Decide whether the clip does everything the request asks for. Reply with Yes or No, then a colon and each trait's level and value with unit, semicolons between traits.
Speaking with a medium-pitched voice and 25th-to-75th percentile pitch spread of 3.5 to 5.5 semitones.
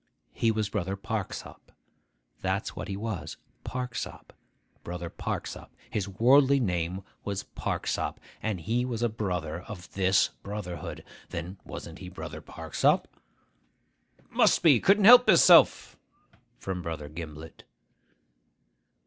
No: low, 100 Hz; average, 4.7 semitones